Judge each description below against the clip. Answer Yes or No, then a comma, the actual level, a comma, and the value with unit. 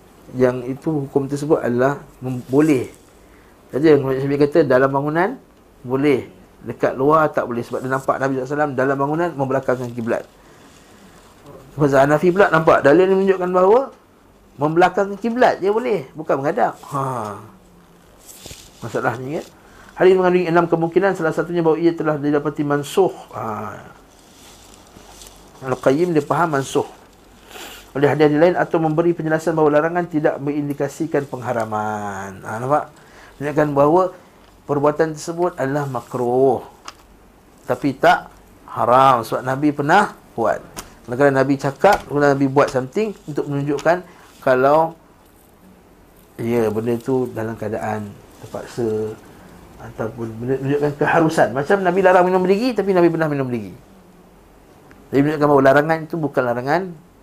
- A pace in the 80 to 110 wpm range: No, average, 130 wpm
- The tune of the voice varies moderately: Yes, average, 4.1 semitones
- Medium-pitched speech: Yes, medium, 145 Hz